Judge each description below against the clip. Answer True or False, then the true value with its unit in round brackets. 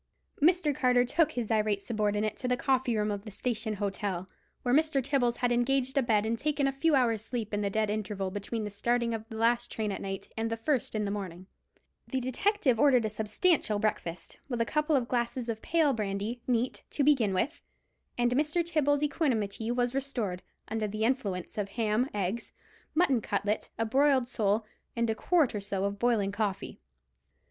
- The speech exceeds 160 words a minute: True (195 wpm)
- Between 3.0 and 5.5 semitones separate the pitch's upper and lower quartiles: True (4.0 semitones)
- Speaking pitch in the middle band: False (230 Hz)